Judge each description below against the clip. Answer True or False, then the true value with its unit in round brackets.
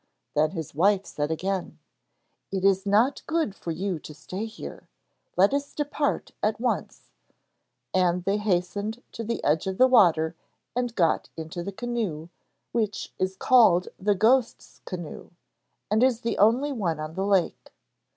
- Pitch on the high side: True (195 Hz)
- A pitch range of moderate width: True (4.9 semitones)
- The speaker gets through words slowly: False (155 wpm)